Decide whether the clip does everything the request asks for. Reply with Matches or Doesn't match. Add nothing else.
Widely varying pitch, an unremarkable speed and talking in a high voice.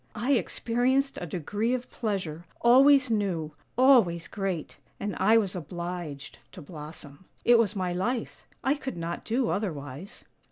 Matches